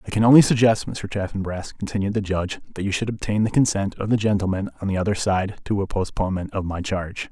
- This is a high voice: No, low, 100 Hz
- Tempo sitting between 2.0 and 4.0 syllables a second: No, 6.5 syllables/s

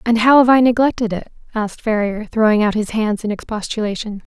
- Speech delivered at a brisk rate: No, average, 195 wpm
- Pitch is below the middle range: No, high, 220 Hz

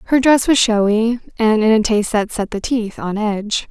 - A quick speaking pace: Yes, fast, 225 wpm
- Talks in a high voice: Yes, high, 220 Hz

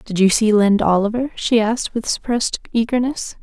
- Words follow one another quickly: No, average, 175 wpm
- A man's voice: No, female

